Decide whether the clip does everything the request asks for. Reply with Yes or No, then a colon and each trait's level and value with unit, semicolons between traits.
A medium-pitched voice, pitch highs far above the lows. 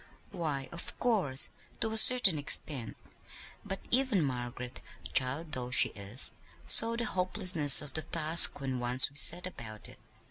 Yes: medium, 150 Hz; wide, 6.4 semitones